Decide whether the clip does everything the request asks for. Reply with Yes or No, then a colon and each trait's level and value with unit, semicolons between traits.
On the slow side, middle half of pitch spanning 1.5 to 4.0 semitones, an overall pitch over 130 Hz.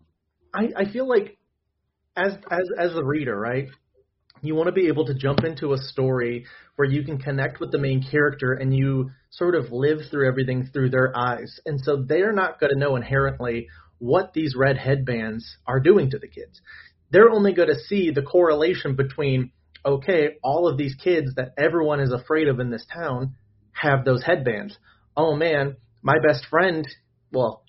No: average, 180 wpm; average, 3.6 semitones; medium, 140 Hz